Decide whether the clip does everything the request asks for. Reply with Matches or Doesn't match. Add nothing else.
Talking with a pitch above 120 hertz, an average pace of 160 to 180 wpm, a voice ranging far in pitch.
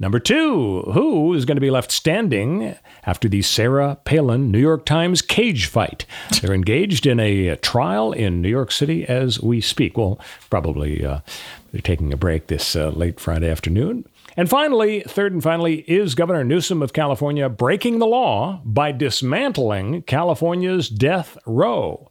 Matches